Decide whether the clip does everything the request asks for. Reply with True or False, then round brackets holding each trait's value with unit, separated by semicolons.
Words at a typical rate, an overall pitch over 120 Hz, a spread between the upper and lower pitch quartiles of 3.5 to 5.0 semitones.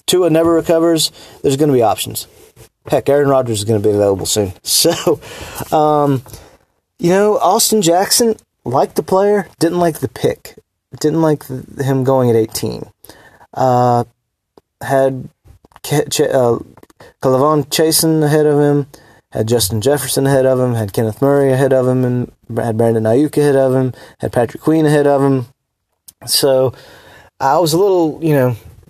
True (160 wpm; 135 Hz; 4.7 semitones)